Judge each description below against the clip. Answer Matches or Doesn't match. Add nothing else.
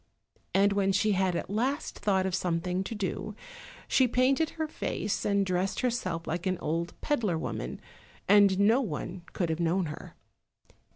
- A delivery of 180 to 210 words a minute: Doesn't match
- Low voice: Doesn't match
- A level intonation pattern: Doesn't match